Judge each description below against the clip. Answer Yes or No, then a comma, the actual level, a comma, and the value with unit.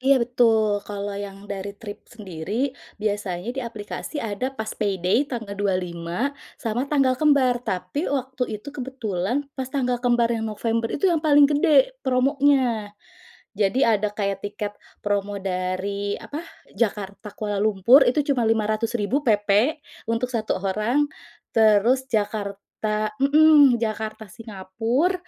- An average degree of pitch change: Yes, average, 3.9 semitones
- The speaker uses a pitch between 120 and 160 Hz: No, high, 220 Hz